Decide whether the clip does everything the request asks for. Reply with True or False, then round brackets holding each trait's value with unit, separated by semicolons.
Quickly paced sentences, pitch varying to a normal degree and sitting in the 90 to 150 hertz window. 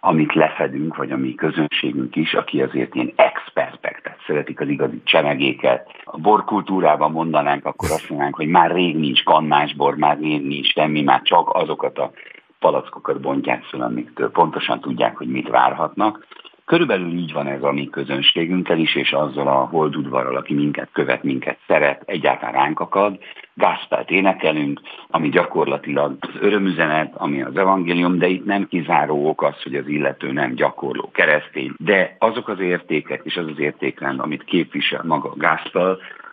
False (160 wpm; 3.8 semitones; 80 Hz)